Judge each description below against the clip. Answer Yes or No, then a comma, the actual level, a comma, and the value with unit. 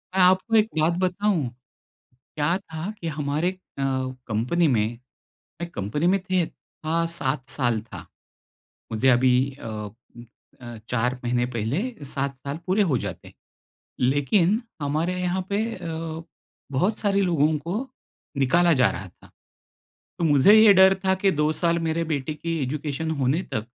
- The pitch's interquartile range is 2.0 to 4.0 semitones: No, wide, 5.6 semitones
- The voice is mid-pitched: Yes, medium, 155 Hz